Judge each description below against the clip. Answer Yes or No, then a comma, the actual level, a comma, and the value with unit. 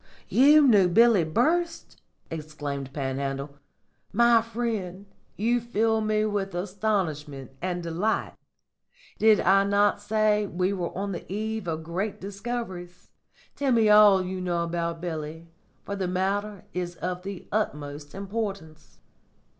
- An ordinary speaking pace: No, slow, 130 wpm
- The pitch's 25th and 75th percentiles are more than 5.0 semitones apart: No, average, 4.2 semitones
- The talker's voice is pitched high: Yes, high, 195 Hz